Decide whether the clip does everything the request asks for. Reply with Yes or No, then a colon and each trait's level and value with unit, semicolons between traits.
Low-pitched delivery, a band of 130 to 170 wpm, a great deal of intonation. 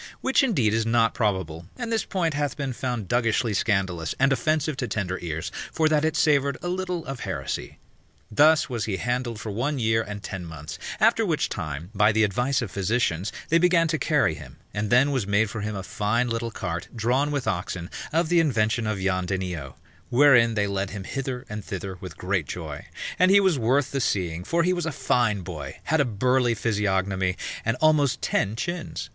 No: low, 115 Hz; average, 200 wpm; wide, 6.3 semitones